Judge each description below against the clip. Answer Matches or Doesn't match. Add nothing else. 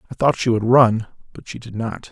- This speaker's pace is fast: Matches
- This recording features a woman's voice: Doesn't match